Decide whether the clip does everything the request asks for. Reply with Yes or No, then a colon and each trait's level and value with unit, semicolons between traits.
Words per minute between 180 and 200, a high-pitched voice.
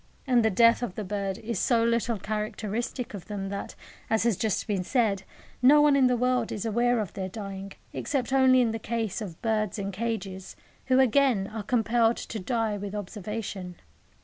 Yes: average, 190 wpm; high, 220 Hz